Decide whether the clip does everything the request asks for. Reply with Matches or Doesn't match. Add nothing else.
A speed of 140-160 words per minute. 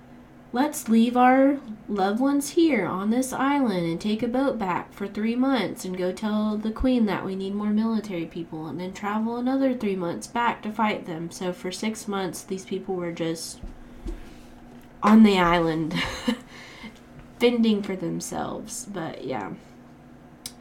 Matches